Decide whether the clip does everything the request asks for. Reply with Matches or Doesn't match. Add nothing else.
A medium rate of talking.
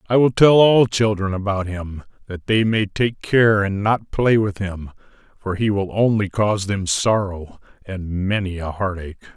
Matches